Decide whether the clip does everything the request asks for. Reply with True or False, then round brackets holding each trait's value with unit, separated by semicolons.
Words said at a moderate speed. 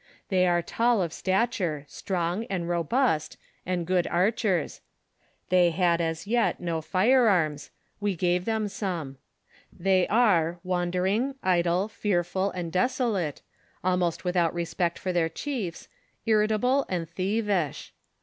False (125 wpm)